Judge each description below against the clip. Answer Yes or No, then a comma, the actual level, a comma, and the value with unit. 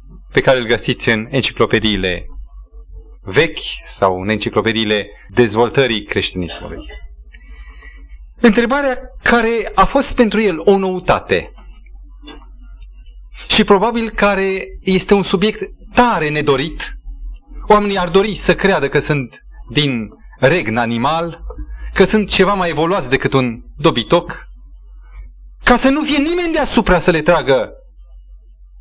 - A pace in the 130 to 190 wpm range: No, slow, 115 wpm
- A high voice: No, medium, 145 Hz